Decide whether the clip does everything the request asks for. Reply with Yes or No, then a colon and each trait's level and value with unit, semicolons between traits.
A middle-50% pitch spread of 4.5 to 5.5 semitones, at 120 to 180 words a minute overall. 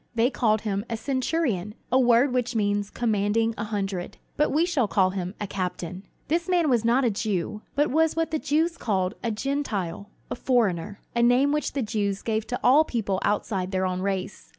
No: average, 4.8 semitones; average, 195 wpm